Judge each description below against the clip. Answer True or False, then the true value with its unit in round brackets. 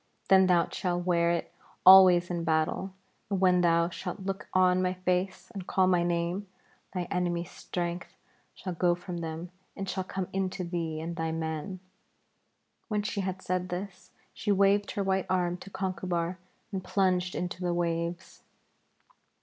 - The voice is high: False (180 Hz)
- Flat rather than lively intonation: True (1.6 semitones)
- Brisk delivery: False (160 wpm)